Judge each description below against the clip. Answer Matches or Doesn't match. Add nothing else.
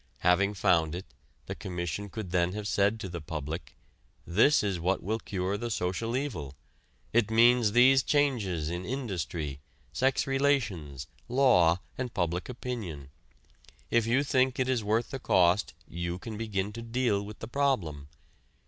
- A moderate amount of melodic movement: Doesn't match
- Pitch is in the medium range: Doesn't match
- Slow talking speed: Doesn't match